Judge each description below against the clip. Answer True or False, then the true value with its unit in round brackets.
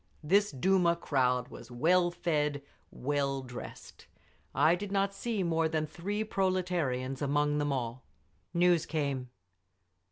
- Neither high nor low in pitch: True (155 Hz)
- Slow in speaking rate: True (125 wpm)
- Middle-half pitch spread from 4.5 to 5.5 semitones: True (4.9 semitones)